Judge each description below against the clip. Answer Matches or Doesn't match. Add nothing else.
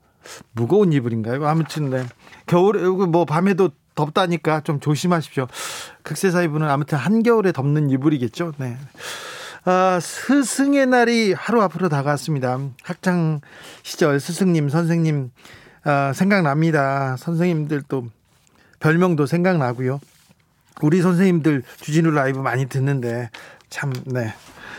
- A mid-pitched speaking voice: Matches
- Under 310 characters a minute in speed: Matches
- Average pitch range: Matches